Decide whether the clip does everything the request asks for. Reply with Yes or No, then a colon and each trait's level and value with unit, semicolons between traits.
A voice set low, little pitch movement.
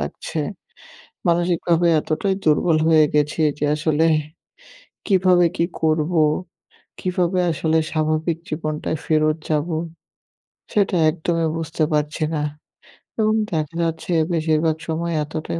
No: medium, 160 Hz; narrow, 1.8 semitones